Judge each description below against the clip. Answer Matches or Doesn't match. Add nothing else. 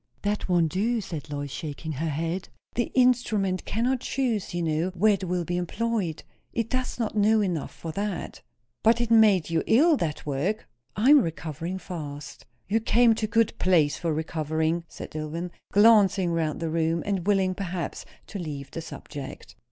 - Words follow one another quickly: Doesn't match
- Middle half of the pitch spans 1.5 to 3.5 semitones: Doesn't match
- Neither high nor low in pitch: Matches